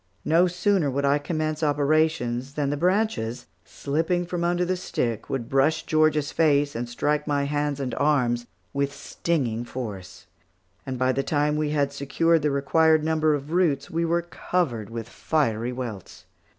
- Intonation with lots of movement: No, average, 3.5 semitones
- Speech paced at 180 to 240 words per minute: No, average, 165 wpm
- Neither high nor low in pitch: Yes, medium, 145 Hz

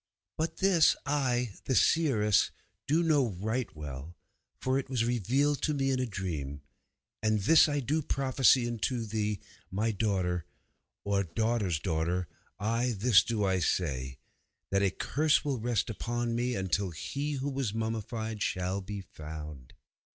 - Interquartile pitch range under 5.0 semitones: No, wide, 5.6 semitones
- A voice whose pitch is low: Yes, low, 110 Hz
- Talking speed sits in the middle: Yes, average, 150 wpm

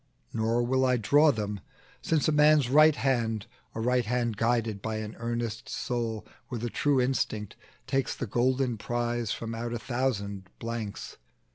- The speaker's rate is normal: Yes, average, 160 wpm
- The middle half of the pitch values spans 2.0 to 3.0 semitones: Yes, narrow, 2.6 semitones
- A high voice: No, low, 120 Hz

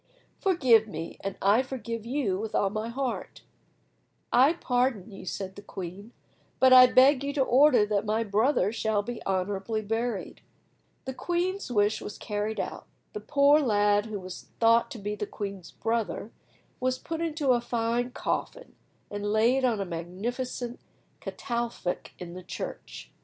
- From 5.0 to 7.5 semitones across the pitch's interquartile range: No, average, 3.9 semitones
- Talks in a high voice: Yes, high, 230 Hz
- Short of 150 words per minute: No, average, 160 wpm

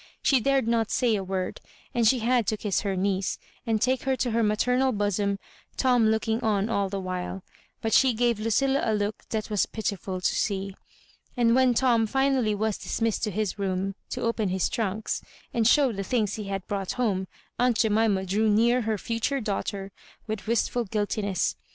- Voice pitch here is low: No, high, 220 Hz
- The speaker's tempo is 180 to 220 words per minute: Yes, average, 190 wpm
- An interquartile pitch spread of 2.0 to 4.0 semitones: Yes, average, 3.0 semitones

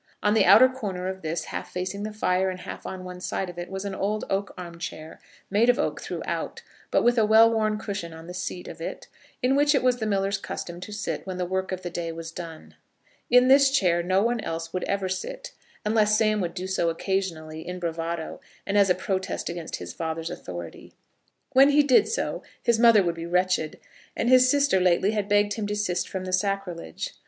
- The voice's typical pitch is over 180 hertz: Yes, high, 190 Hz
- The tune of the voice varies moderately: Yes, average, 3.5 semitones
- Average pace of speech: No, fast, 220 wpm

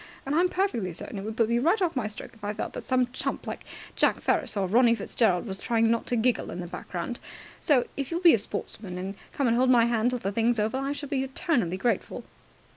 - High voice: Yes, high, 235 Hz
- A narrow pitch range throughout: No, average, 4.1 semitones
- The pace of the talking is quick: Yes, fast, 255 wpm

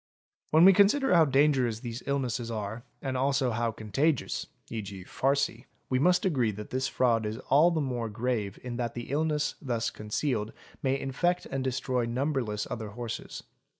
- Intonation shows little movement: No, average, 3.6 semitones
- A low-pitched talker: Yes, low, 125 Hz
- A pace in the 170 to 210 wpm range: Yes, average, 175 wpm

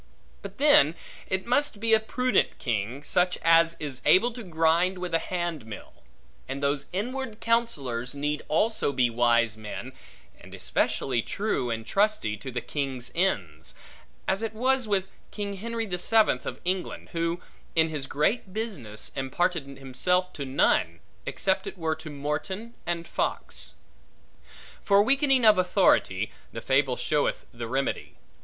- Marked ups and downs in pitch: Yes, wide, 7.4 semitones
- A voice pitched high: No, medium, 165 Hz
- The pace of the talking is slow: No, average, 150 wpm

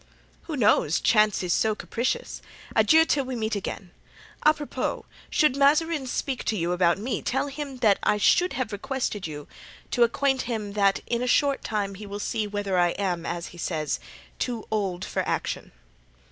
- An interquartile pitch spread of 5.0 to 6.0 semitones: Yes, wide, 5.4 semitones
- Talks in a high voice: Yes, high, 220 Hz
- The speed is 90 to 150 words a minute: No, average, 175 wpm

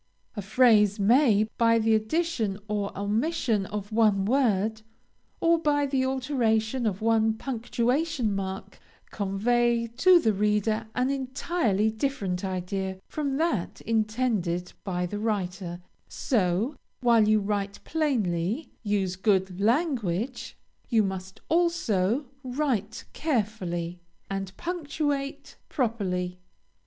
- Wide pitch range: No, average, 4.9 semitones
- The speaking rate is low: Yes, slow, 110 wpm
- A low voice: No, high, 220 Hz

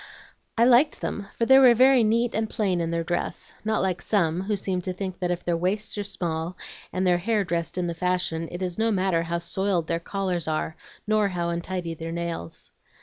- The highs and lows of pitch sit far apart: No, average, 3.4 semitones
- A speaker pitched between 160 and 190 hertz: Yes, medium, 185 Hz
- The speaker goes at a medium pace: No, fast, 215 wpm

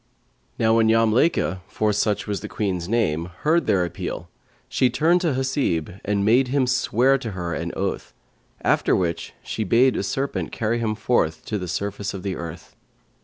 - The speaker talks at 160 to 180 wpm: Yes, average, 175 wpm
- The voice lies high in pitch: No, low, 110 Hz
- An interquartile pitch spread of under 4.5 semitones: No, average, 5.2 semitones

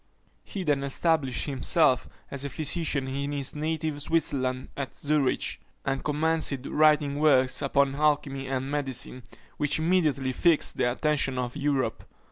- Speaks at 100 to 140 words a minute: Yes, slow, 135 wpm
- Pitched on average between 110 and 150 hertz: Yes, medium, 140 Hz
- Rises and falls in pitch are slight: Yes, narrow, 2.3 semitones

